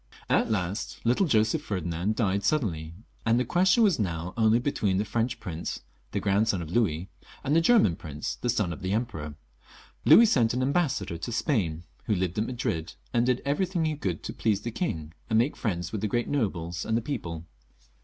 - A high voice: No, low, 110 Hz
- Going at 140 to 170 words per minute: No, average, 195 wpm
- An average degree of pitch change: No, wide, 6.0 semitones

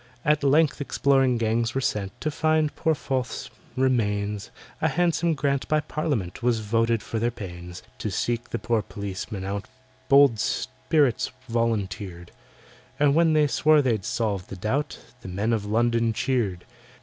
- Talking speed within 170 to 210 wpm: No, average, 150 wpm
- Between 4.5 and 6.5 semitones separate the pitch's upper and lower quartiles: Yes, wide, 5.4 semitones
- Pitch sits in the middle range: No, low, 115 Hz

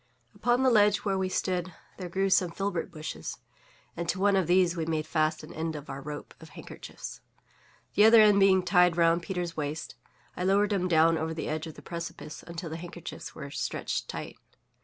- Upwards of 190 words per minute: Yes, average, 200 wpm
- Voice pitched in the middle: Yes, medium, 175 Hz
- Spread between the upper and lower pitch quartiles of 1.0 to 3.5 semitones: Yes, average, 3.1 semitones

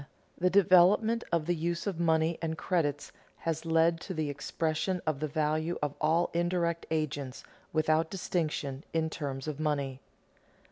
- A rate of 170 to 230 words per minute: No, average, 150 wpm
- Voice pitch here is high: No, medium, 160 Hz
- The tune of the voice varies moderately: No, narrow, 2.1 semitones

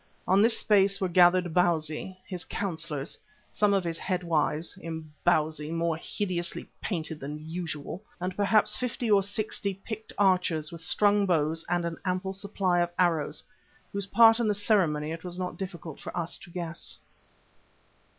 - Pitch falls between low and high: Yes, medium, 175 Hz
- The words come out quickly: No, average, 160 wpm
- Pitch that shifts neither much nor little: Yes, average, 3.4 semitones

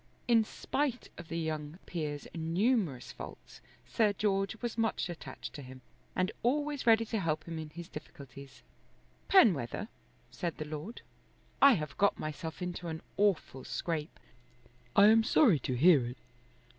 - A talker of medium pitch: Yes, medium, 175 Hz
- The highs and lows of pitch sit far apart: Yes, wide, 6.3 semitones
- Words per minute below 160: Yes, average, 150 wpm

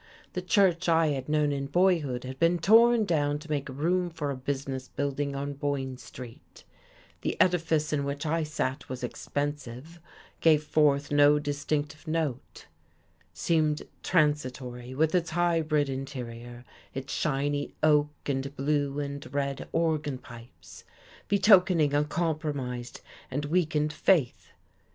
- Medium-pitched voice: Yes, medium, 145 Hz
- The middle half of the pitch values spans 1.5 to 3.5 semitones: Yes, average, 2.9 semitones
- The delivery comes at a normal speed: No, slow, 130 wpm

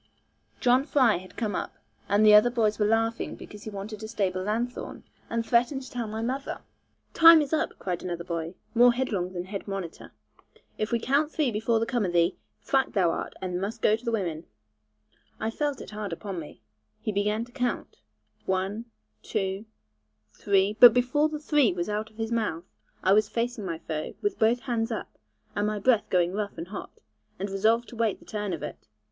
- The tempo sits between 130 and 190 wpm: No, average, 200 wpm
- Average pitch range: Yes, average, 3.7 semitones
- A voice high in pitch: Yes, high, 215 Hz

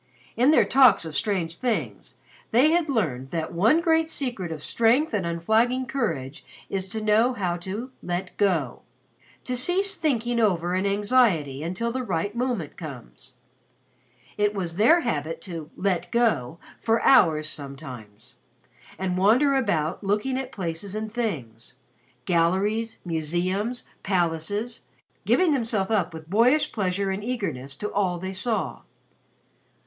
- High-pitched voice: Yes, high, 200 Hz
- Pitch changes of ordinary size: No, wide, 6.1 semitones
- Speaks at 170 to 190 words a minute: No, average, 140 wpm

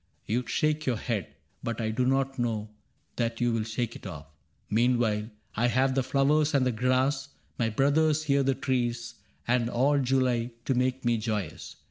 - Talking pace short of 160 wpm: No, average, 180 wpm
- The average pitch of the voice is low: Yes, low, 125 Hz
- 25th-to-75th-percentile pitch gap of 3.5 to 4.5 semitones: No, average, 2.7 semitones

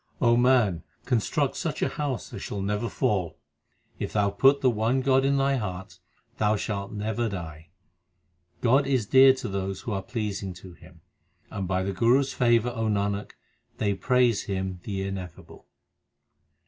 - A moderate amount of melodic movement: Yes, average, 4.3 semitones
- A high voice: No, low, 105 Hz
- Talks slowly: No, average, 165 wpm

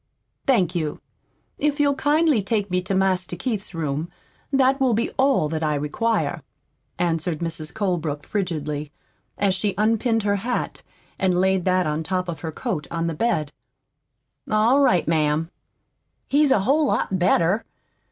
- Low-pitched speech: No, medium, 185 Hz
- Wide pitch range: Yes, wide, 5.8 semitones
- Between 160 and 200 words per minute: No, average, 150 wpm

